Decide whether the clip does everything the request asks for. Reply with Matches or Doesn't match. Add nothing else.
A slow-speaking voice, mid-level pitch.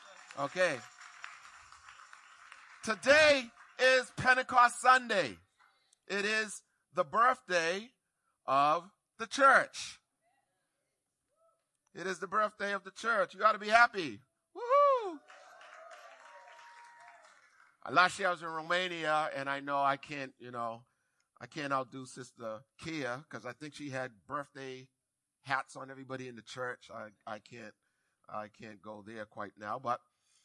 Matches